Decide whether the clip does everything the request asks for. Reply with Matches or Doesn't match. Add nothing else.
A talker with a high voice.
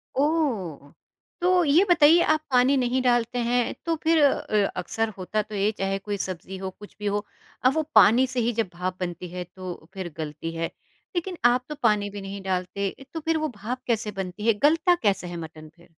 Matches